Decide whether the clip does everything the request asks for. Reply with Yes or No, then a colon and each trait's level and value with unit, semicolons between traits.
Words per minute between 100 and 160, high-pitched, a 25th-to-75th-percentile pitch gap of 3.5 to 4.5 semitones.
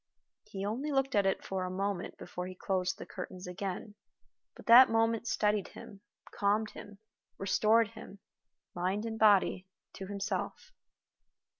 No: average, 145 wpm; high, 200 Hz; average, 2.7 semitones